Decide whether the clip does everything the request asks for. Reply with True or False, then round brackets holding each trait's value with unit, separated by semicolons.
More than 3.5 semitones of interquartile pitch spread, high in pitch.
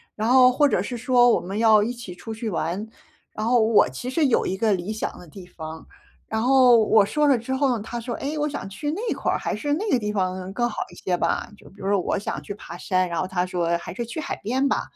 True (5.0 semitones; 220 Hz)